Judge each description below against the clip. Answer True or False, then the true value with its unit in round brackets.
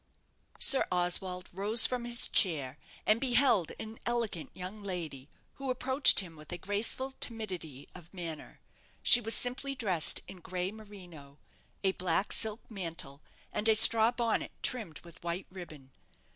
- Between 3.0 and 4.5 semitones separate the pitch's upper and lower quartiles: False (5.1 semitones)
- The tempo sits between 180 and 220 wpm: False (145 wpm)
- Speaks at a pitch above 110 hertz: True (190 Hz)